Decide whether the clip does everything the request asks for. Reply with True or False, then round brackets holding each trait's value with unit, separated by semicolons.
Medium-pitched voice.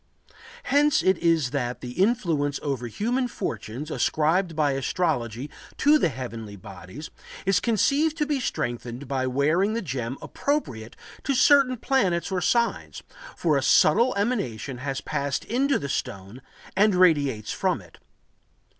True (155 Hz)